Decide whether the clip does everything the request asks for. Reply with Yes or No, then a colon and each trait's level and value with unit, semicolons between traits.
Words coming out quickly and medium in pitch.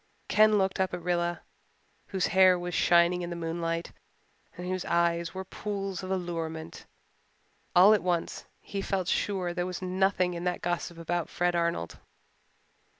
No: average, 155 wpm; medium, 180 Hz